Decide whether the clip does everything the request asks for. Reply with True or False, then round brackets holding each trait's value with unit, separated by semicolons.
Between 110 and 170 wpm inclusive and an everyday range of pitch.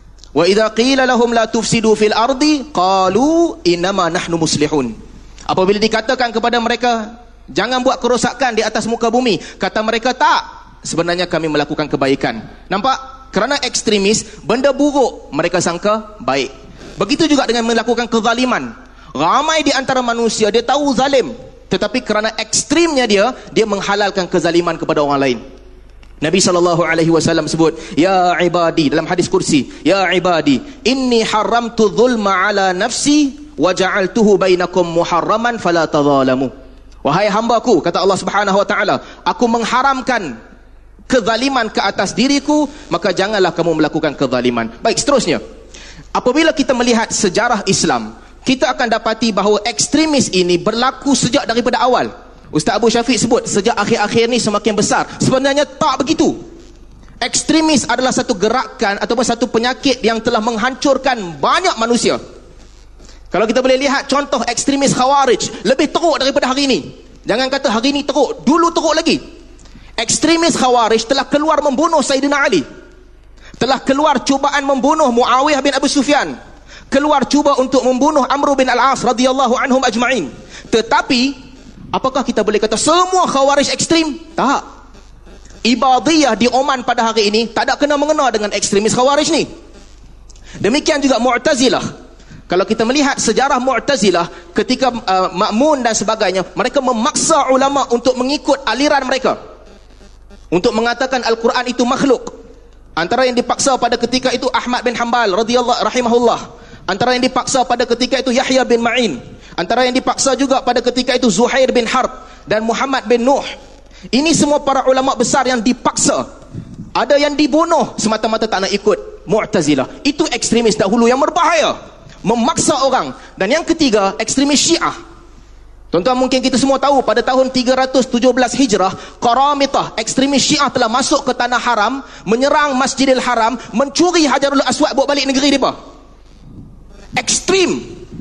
True (140 wpm; 4.5 semitones)